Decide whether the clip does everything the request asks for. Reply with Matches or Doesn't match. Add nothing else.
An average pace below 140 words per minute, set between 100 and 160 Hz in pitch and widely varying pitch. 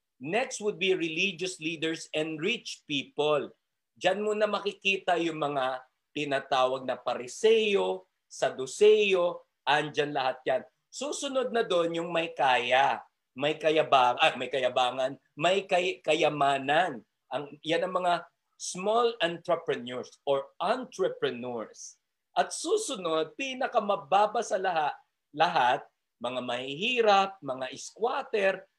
Doesn't match